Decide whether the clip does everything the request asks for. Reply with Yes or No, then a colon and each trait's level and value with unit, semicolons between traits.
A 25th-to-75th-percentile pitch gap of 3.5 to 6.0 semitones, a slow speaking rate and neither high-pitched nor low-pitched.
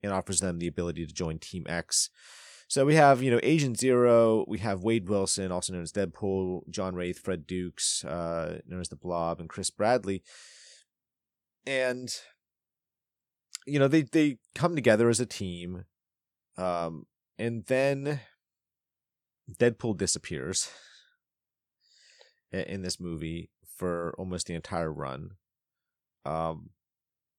No: wide, 5.6 semitones; slow, 130 wpm; very low, 95 Hz